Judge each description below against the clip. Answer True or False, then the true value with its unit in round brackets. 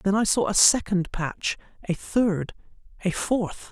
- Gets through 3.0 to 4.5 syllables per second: True (3.9 syllables/s)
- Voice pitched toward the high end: True (195 Hz)